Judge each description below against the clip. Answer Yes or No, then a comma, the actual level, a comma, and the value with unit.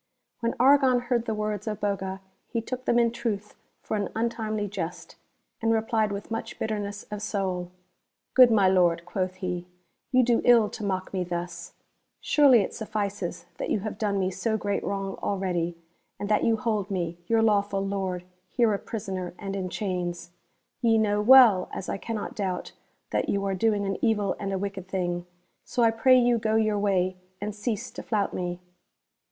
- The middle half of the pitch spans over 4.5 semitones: No, average, 3.1 semitones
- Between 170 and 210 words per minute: Yes, average, 190 wpm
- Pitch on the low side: No, high, 205 Hz